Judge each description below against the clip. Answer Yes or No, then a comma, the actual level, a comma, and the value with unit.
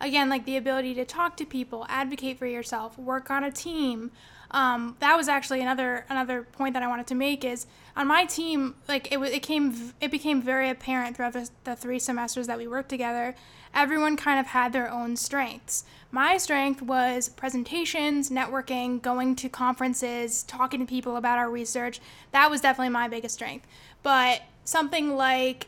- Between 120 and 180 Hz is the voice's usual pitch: No, very high, 260 Hz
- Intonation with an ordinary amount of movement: No, narrow, 2.0 semitones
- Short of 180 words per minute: No, average, 185 wpm